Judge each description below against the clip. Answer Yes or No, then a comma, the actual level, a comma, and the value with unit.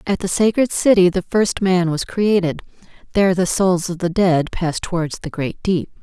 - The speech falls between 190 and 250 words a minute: Yes, average, 200 wpm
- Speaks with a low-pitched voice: No, medium, 185 Hz